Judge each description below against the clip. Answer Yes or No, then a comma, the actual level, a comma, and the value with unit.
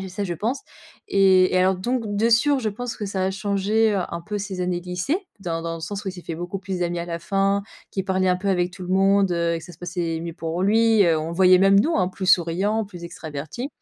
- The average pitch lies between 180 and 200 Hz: Yes, high, 190 Hz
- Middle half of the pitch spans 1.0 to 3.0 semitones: Yes, narrow, 2.5 semitones